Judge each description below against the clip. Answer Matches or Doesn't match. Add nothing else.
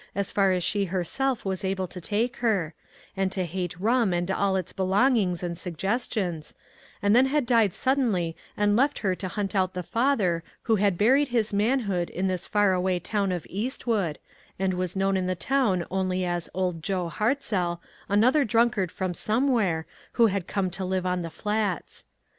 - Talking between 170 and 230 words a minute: Matches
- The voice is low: Doesn't match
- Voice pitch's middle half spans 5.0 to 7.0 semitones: Doesn't match